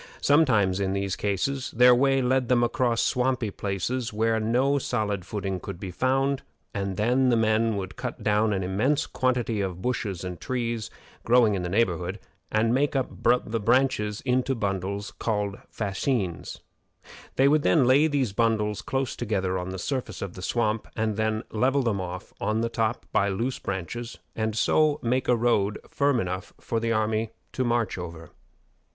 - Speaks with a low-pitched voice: Yes, low, 115 Hz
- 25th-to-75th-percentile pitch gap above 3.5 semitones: Yes, average, 4.2 semitones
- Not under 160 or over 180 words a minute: Yes, average, 170 wpm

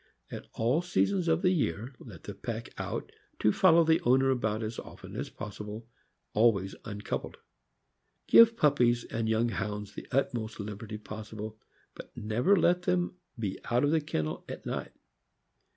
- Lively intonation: Yes, wide, 6.6 semitones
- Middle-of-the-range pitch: No, low, 115 Hz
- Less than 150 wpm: No, average, 160 wpm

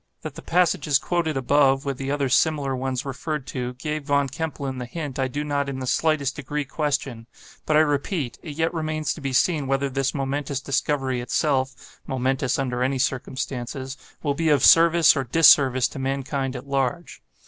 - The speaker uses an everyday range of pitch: No, narrow, 2.3 semitones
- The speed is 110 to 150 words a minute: No, average, 180 wpm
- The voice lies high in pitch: No, medium, 140 Hz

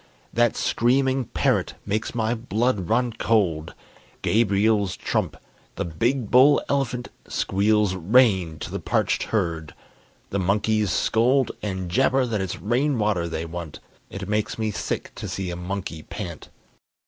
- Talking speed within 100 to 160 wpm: Yes, average, 140 wpm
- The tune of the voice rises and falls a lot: No, average, 4.4 semitones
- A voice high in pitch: No, low, 105 Hz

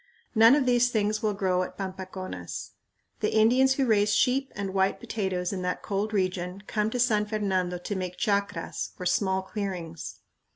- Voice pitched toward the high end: Yes, high, 200 Hz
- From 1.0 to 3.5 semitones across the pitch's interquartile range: Yes, average, 2.8 semitones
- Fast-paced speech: No, average, 170 wpm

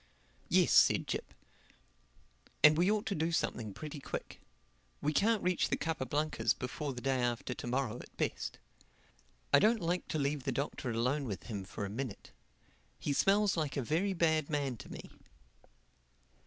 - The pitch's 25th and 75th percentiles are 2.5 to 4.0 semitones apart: No, average, 4.9 semitones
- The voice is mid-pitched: Yes, medium, 145 Hz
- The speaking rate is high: No, average, 170 wpm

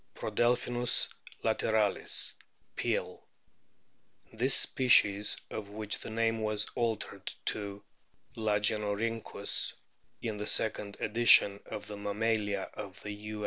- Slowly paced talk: Yes, slow, 105 wpm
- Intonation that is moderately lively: No, narrow, 1.7 semitones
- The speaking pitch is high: No, low, 105 Hz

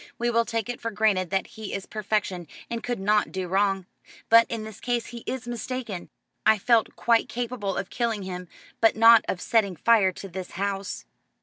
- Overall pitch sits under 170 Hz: No, high, 215 Hz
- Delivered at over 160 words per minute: Yes, average, 195 wpm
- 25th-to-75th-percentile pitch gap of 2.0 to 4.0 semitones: Yes, average, 3.2 semitones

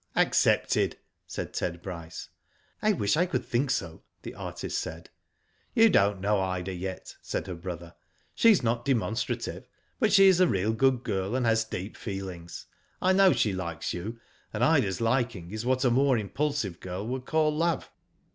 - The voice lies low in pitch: Yes, low, 110 Hz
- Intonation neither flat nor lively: No, wide, 6.5 semitones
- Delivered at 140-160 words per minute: No, average, 175 wpm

